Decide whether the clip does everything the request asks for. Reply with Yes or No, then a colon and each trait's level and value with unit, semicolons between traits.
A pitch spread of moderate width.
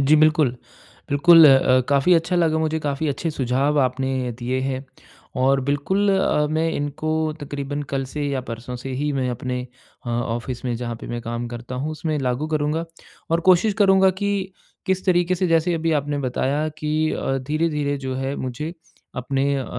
Yes: average, 3.5 semitones